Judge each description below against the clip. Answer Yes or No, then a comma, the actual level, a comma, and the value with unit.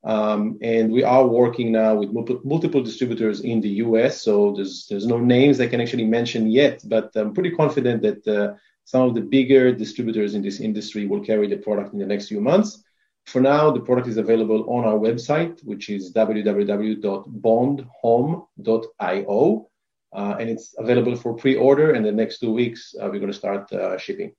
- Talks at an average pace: Yes, average, 185 wpm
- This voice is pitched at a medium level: No, low, 115 Hz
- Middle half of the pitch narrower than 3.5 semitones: Yes, average, 2.9 semitones